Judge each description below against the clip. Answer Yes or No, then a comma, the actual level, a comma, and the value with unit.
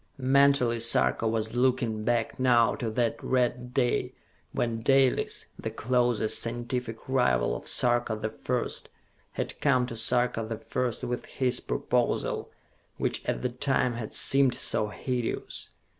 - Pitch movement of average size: No, narrow, 1.9 semitones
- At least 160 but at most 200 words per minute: No, average, 140 wpm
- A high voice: No, low, 120 Hz